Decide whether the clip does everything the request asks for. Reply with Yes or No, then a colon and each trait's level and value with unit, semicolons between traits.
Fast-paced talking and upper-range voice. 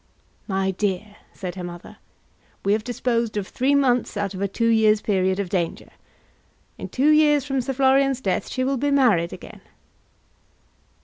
No: average, 170 wpm; high, 220 Hz